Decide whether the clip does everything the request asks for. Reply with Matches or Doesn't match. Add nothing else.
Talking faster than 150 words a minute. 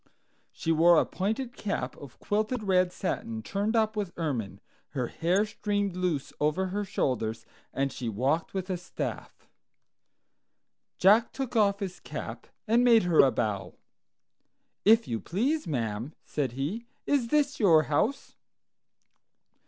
Doesn't match